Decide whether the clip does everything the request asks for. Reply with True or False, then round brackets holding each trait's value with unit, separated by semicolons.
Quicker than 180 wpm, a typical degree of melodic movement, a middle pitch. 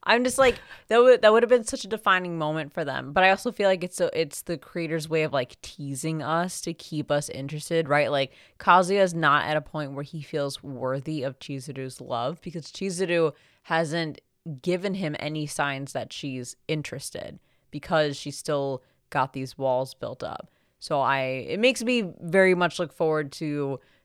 True (190 wpm; 4.2 semitones; 155 Hz)